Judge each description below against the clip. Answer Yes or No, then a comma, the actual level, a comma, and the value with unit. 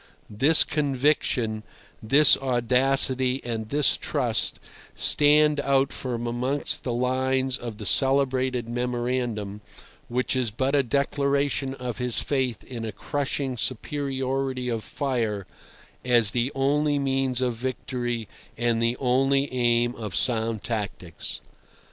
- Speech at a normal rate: No, slow, 120 wpm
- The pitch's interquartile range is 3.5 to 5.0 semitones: No, narrow, 2.4 semitones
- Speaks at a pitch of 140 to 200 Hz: No, low, 130 Hz